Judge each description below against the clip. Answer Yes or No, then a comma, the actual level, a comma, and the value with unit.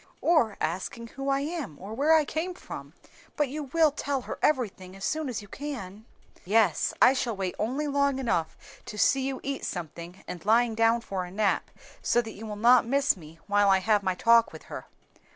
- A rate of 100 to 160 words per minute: No, fast, 205 wpm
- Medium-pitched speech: No, high, 230 Hz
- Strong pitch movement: Yes, wide, 6.0 semitones